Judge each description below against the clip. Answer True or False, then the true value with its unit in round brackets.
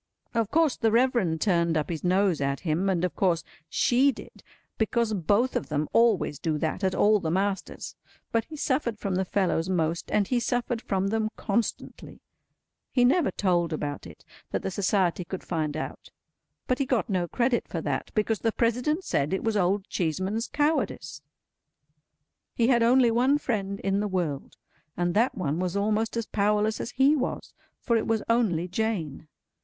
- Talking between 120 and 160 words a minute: False (175 wpm)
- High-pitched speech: True (205 Hz)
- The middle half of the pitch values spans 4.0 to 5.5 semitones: True (5.0 semitones)